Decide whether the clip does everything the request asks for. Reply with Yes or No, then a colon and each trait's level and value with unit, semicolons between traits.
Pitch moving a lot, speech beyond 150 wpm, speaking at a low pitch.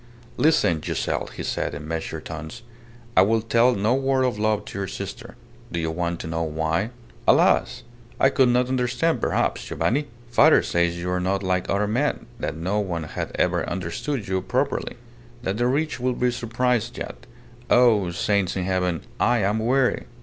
Yes: wide, 6.2 semitones; average, 180 wpm; low, 105 Hz